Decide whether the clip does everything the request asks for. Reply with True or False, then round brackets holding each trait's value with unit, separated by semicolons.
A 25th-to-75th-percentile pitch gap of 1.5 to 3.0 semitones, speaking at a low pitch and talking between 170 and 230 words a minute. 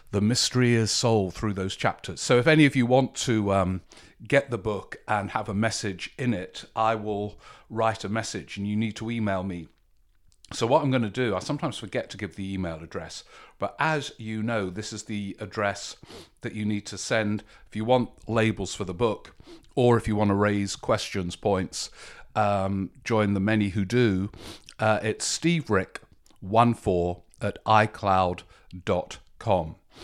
True (2.7 semitones; 110 Hz; 180 wpm)